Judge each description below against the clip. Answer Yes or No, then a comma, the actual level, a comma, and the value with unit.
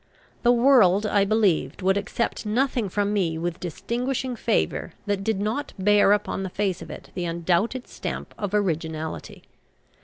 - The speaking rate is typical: Yes, average, 155 wpm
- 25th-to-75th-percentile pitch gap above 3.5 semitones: Yes, average, 3.9 semitones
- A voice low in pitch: No, high, 205 Hz